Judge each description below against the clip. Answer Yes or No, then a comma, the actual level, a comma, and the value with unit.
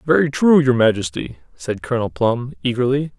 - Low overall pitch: Yes, low, 125 Hz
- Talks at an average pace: Yes, average, 150 wpm